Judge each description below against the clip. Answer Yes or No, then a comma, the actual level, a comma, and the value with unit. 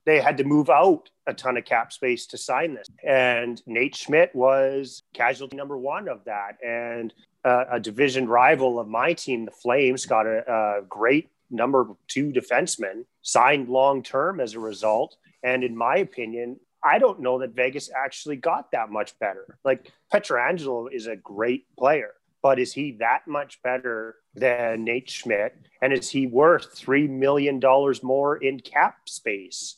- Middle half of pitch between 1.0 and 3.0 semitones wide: Yes, average, 2.7 semitones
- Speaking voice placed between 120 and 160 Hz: Yes, low, 130 Hz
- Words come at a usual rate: Yes, average, 170 wpm